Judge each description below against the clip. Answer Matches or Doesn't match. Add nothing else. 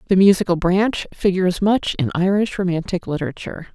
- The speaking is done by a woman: Matches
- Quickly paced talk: Doesn't match